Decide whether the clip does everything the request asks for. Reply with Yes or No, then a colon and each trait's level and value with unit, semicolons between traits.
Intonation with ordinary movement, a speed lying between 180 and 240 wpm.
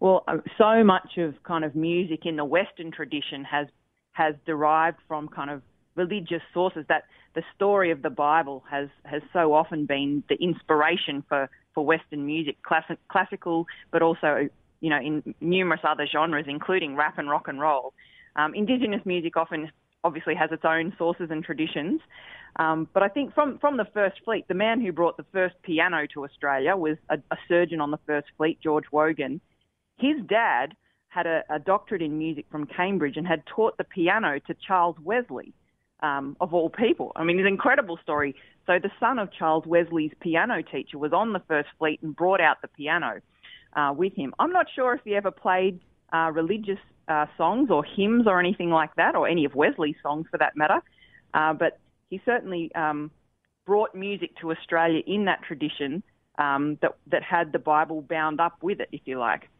Yes: average, 3.4 semitones; average, 190 wpm